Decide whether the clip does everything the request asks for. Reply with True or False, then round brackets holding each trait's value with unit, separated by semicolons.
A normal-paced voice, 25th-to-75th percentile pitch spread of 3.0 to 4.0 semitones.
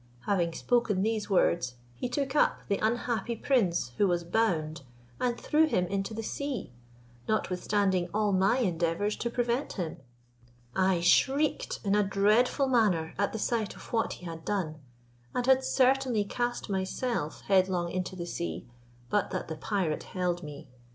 False (160 wpm; 5.3 semitones)